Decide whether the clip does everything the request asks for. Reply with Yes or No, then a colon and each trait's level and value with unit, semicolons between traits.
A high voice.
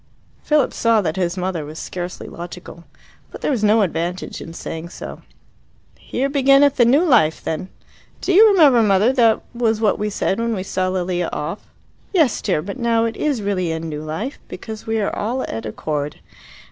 Yes: high, 205 Hz